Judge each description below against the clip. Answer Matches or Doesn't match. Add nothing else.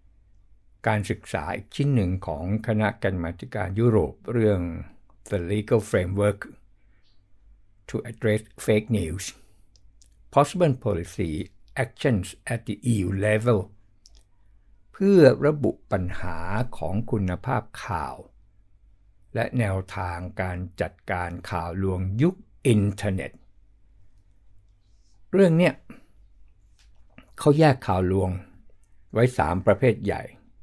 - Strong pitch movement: Doesn't match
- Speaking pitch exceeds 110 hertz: Doesn't match